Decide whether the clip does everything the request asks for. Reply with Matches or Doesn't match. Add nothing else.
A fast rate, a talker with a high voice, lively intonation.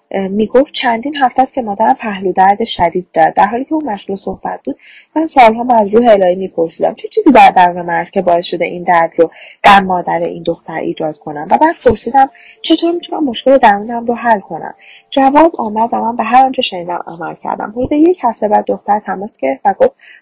Matches